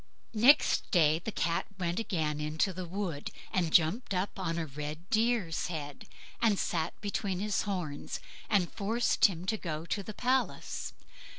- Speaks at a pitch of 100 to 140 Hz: No, medium, 180 Hz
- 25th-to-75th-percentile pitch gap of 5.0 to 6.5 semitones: No, average, 4.3 semitones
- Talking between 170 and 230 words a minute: No, average, 160 wpm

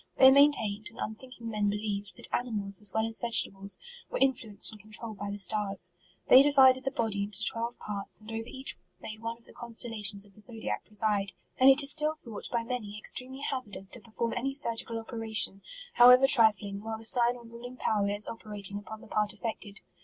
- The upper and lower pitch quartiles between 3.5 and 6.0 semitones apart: No, average, 2.9 semitones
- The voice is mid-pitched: No, high, 225 Hz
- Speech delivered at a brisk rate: Yes, fast, 215 wpm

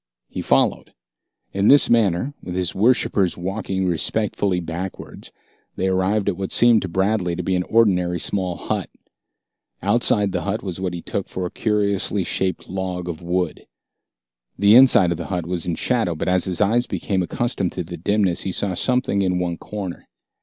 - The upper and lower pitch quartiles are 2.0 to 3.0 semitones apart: Yes, narrow, 2.5 semitones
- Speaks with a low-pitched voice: Yes, very low, 95 Hz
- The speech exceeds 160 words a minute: Yes, average, 180 wpm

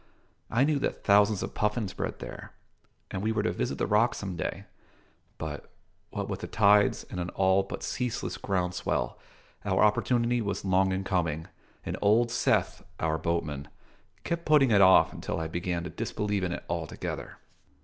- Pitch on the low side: Yes, low, 100 Hz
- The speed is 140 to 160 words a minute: No, average, 175 wpm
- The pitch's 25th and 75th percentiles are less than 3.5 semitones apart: No, average, 3.8 semitones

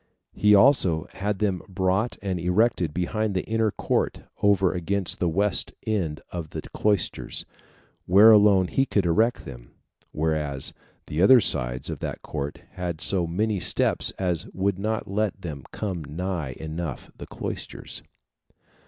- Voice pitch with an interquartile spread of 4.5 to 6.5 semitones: No, average, 4.1 semitones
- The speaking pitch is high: No, very low, 95 Hz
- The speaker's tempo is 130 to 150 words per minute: Yes, average, 145 wpm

